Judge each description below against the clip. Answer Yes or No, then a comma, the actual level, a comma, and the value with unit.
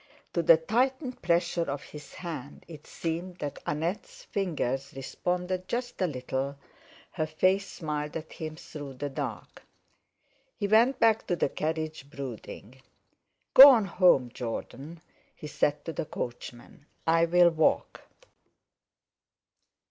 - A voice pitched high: No, medium, 160 Hz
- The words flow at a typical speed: No, slow, 125 wpm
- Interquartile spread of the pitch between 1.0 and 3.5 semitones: No, average, 4.3 semitones